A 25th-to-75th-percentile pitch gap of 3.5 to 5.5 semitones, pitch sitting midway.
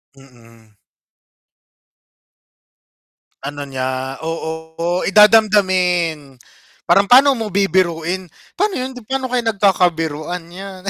Yes: average, 4.9 semitones; medium, 175 Hz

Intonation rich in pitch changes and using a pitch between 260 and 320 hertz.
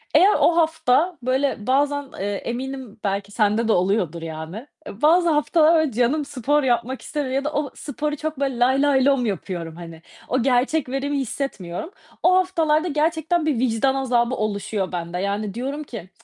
Yes: wide, 5.8 semitones; very high, 265 Hz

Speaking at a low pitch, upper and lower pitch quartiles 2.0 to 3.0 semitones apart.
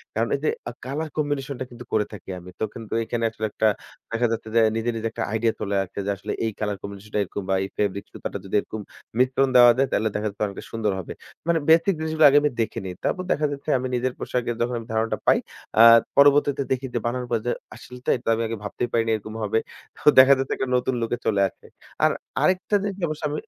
No: low, 120 Hz; average, 3.9 semitones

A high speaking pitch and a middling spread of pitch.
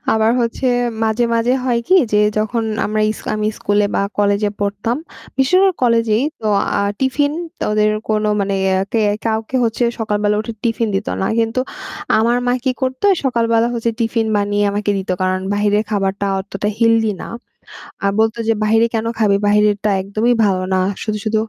No: high, 220 Hz; narrow, 2.1 semitones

